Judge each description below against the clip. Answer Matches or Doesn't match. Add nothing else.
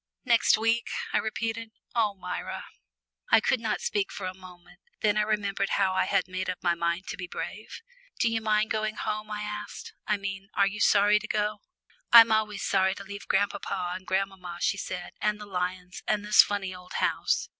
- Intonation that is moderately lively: Doesn't match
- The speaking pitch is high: Matches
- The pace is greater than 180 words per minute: Matches